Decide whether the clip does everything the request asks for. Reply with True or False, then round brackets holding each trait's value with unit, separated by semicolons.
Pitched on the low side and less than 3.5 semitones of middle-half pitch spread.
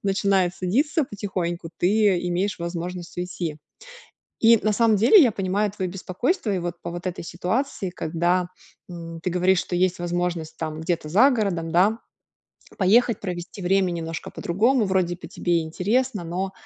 False (185 Hz; 2.9 semitones)